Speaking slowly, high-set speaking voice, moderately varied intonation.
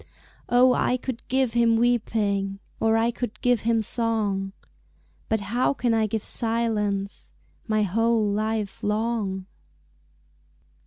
No: slow, 120 wpm; high, 225 Hz; narrow, 2.1 semitones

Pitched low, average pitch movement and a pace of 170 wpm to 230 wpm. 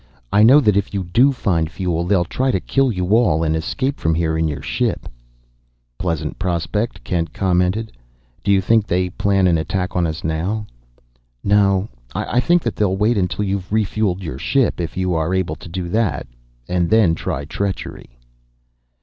Yes: very low, 95 Hz; average, 3.7 semitones; average, 180 wpm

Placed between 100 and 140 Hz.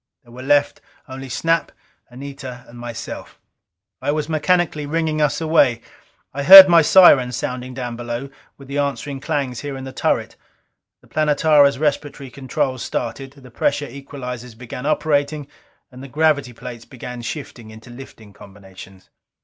Yes: low, 135 Hz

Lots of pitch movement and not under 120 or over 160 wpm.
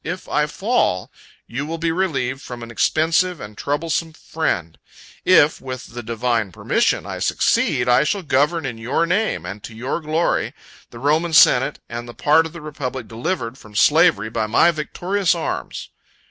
No: wide, 5.8 semitones; average, 170 wpm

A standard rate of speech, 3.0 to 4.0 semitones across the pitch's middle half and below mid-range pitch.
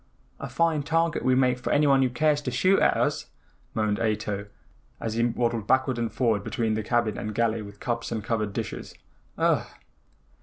Yes: average, 185 wpm; average, 3.3 semitones; low, 120 Hz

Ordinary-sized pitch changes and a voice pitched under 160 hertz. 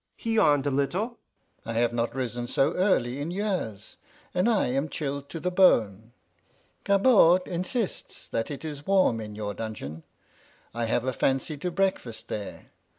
No: wide, 7.7 semitones; medium, 140 Hz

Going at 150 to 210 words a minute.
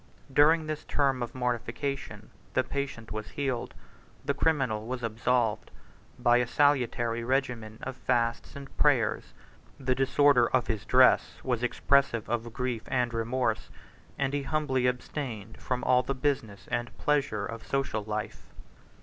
No: average, 140 wpm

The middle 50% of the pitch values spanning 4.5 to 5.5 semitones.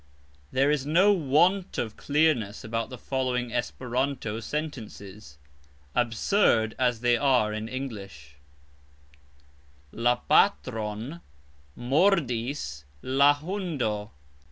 Yes: average, 4.8 semitones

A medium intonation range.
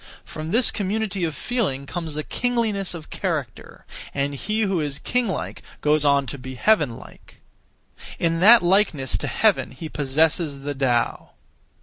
No: wide, 6.0 semitones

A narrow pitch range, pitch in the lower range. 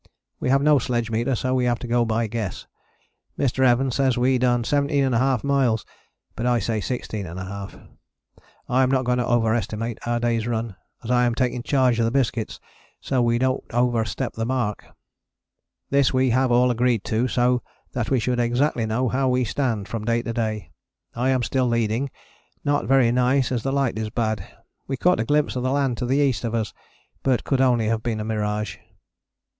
Yes: narrow, 2.3 semitones; low, 120 Hz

